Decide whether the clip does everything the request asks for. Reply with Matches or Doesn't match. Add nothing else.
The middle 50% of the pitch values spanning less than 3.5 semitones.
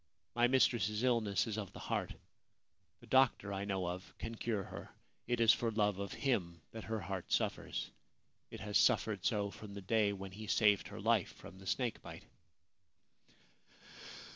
Matches